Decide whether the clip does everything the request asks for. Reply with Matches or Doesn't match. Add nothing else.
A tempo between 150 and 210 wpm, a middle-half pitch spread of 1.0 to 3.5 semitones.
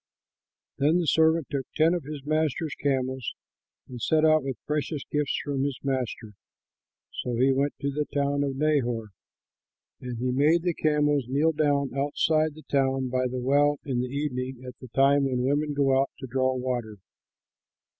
Matches